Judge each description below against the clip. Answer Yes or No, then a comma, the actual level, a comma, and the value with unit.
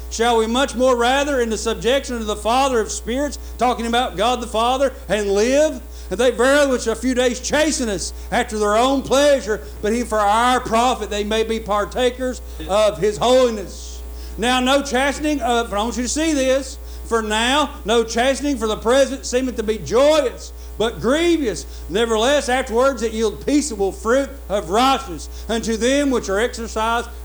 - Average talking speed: Yes, average, 180 wpm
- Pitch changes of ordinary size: Yes, average, 3.6 semitones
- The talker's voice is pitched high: Yes, high, 235 Hz